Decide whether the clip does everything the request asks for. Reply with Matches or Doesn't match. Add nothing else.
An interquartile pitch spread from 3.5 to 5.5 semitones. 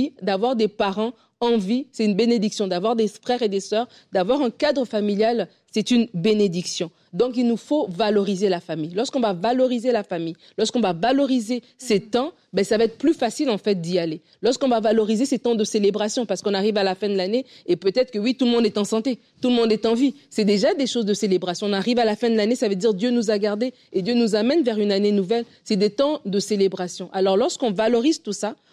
Doesn't match